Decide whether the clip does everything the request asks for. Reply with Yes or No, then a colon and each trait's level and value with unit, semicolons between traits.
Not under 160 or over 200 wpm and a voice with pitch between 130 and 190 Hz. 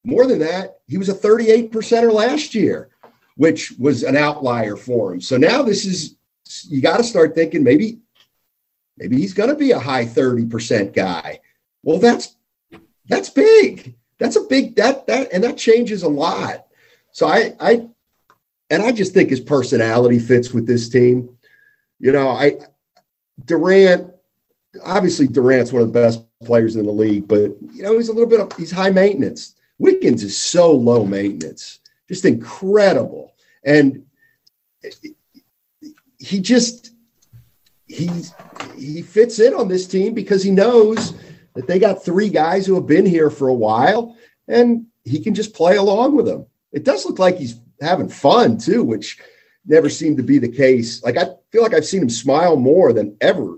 Yes: average, 170 wpm; medium, 185 Hz